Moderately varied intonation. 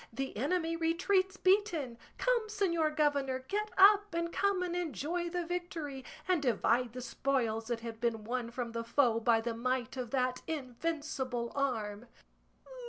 No: wide, 6.5 semitones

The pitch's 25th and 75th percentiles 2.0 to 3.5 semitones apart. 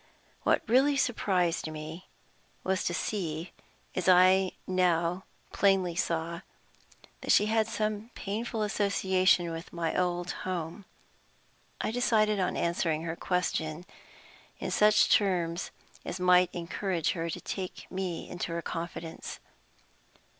Yes: average, 2.8 semitones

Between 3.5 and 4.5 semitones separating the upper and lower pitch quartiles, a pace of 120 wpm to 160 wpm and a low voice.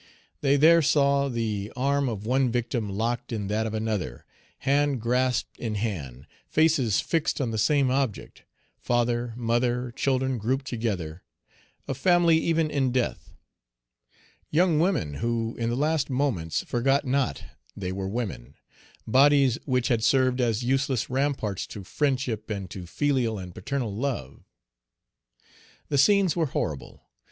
Yes: average, 4.2 semitones; average, 140 wpm; low, 125 Hz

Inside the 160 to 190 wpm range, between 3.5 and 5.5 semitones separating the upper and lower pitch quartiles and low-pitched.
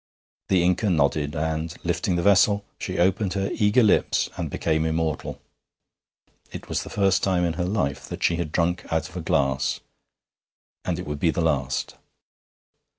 No: average, 170 wpm; average, 3.0 semitones; very low, 85 Hz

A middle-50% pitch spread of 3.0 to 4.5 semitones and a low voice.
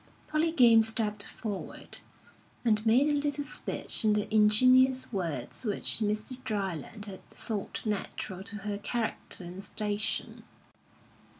No: average, 3.4 semitones; high, 215 Hz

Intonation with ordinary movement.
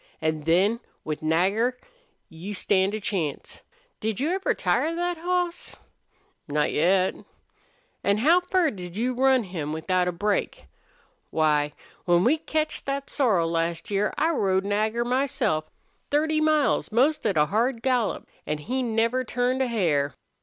No: wide, 7.4 semitones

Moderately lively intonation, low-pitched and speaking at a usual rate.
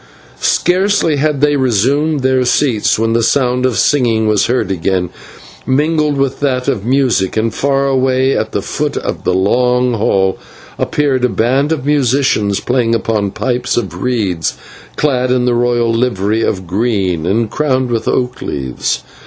Yes: average, 4.0 semitones; low, 125 Hz; average, 160 wpm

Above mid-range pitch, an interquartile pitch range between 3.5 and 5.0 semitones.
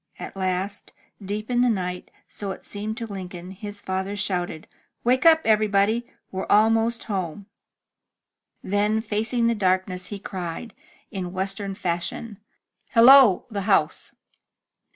No: high, 200 Hz; average, 2.9 semitones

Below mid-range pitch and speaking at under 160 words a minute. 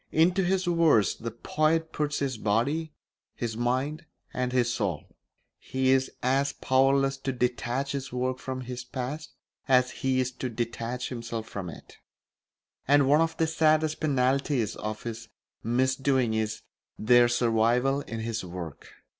Yes: low, 130 Hz; average, 145 wpm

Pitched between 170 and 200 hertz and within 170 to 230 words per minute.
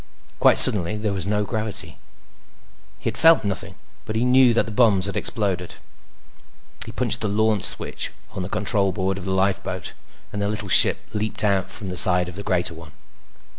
No: low, 100 Hz; average, 190 wpm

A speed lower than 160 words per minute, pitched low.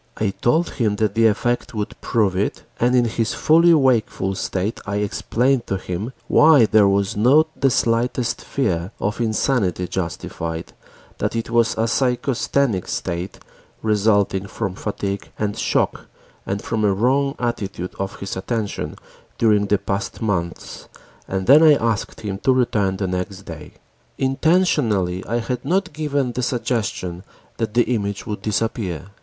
Yes: average, 150 wpm; low, 110 Hz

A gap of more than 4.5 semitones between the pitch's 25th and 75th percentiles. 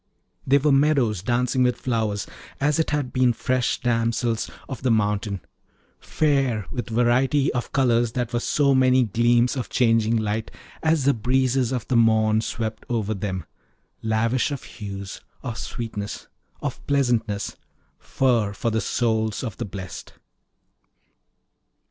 No: average, 2.8 semitones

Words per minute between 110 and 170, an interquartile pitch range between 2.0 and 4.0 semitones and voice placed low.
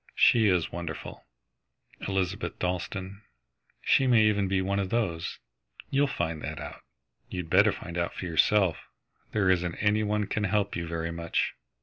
Yes: average, 155 wpm; average, 3.3 semitones; very low, 95 Hz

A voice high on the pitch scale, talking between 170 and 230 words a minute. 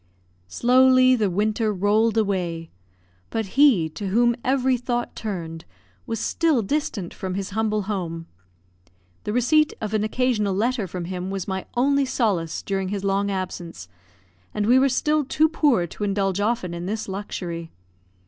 No: high, 210 Hz; average, 155 wpm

